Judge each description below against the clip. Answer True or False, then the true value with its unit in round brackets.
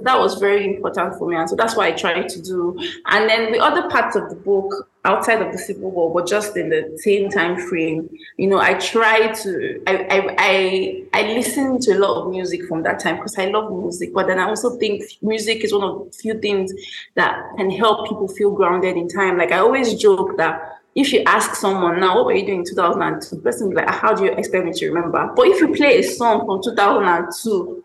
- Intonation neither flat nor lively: True (3.1 semitones)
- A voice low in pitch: False (200 Hz)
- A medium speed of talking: False (250 wpm)